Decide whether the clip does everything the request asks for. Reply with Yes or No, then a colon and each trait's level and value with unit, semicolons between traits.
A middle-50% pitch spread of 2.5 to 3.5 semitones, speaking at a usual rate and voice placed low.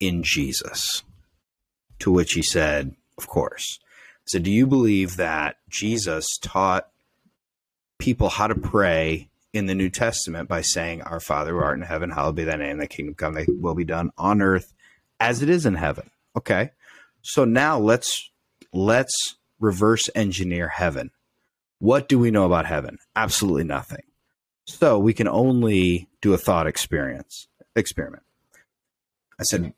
No: average, 4.6 semitones; average, 155 wpm; very low, 95 Hz